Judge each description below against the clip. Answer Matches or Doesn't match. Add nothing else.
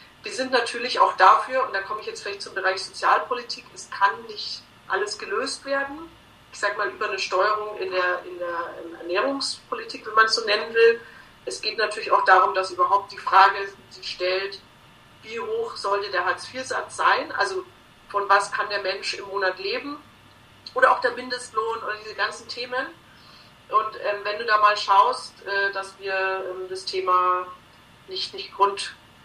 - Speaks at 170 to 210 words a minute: Matches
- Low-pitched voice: Doesn't match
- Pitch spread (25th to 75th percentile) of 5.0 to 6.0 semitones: Matches